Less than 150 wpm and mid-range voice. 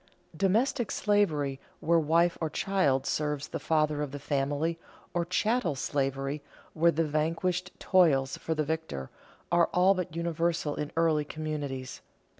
Yes: average, 140 wpm; medium, 160 Hz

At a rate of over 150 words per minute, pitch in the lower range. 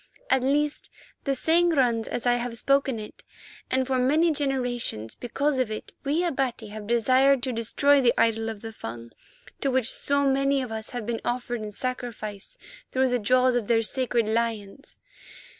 No: average, 175 wpm; high, 245 Hz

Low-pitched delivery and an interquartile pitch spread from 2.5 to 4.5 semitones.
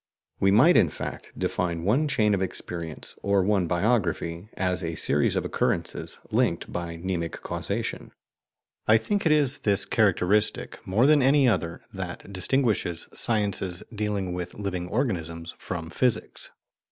Yes: very low, 95 Hz; average, 4.2 semitones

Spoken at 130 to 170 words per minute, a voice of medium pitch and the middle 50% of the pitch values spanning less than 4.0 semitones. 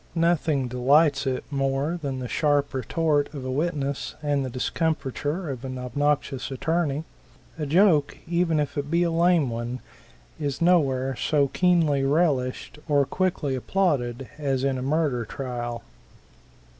Yes: average, 145 wpm; medium, 145 Hz; average, 3.5 semitones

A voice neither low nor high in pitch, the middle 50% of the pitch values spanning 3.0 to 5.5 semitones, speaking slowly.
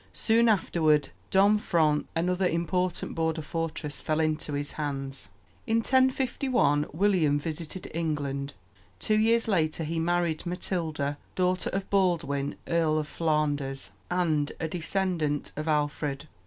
Yes: medium, 160 Hz; average, 3.6 semitones; slow, 120 wpm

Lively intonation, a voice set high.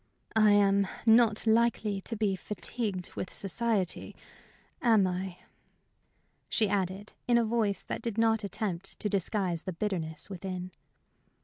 No: average, 3.0 semitones; high, 200 Hz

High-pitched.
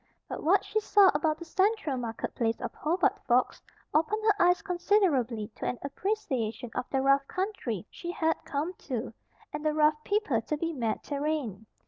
Yes: very high, 300 Hz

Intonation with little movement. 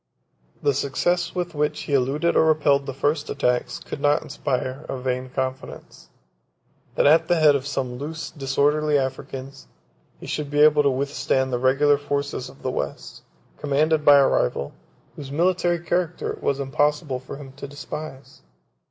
Yes: narrow, 2.2 semitones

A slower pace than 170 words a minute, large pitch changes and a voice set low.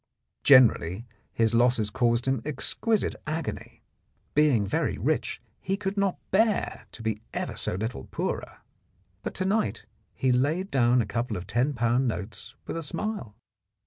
Yes: average, 150 wpm; wide, 6.5 semitones; low, 125 Hz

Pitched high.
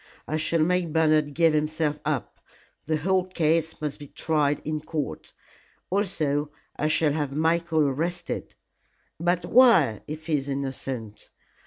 No: medium, 155 Hz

